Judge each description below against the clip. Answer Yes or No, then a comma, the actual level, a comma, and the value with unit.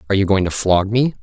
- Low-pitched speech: Yes, low, 100 Hz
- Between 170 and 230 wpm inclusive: No, fast, 295 wpm